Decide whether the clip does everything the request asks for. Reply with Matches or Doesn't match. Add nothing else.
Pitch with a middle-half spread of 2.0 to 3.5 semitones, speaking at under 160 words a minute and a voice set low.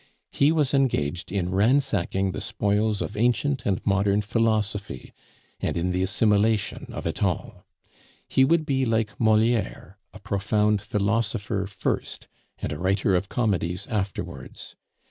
Matches